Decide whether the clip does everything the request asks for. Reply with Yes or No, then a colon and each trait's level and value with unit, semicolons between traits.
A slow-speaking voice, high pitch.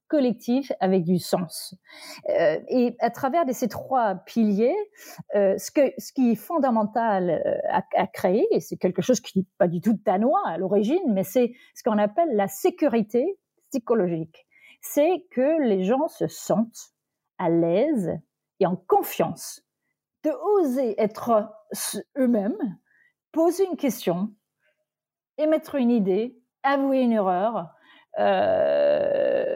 Yes: slow, 135 wpm; high, 245 Hz